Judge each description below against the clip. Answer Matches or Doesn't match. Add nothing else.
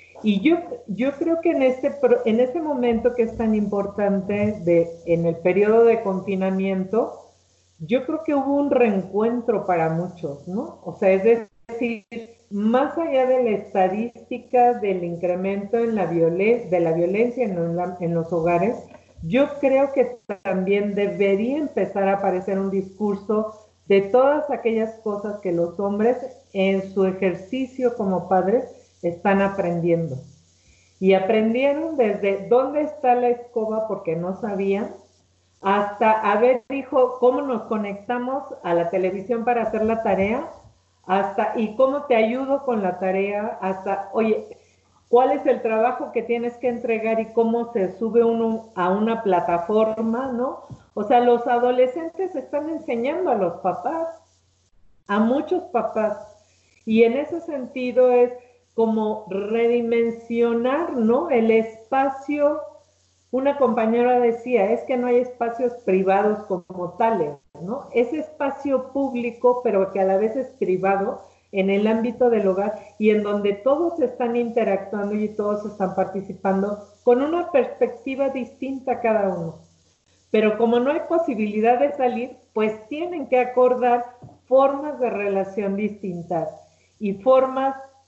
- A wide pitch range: Doesn't match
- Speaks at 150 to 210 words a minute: Doesn't match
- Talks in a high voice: Matches